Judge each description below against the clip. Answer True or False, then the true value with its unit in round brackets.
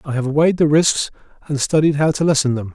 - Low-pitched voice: False (145 Hz)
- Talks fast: True (240 wpm)